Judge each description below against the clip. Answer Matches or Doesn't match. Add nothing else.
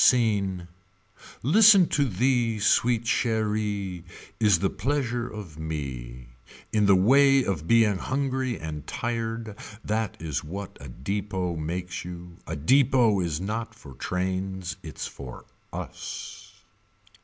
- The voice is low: Matches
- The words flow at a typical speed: Doesn't match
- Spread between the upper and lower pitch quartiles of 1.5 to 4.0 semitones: Doesn't match